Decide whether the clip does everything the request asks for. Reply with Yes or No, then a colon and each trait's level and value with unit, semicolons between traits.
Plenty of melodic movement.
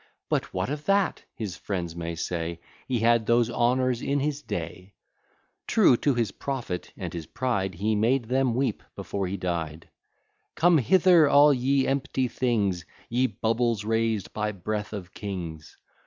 Yes: wide, 5.9 semitones